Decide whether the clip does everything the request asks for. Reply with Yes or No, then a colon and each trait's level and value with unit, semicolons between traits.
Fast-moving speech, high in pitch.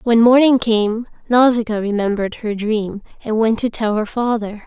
No: average, 165 wpm; high, 225 Hz